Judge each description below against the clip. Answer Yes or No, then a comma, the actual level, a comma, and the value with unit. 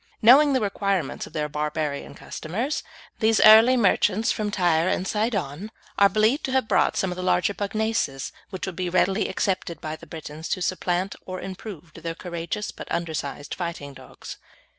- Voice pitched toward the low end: No, medium, 185 Hz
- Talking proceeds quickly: No, average, 170 wpm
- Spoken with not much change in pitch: No, average, 4.7 semitones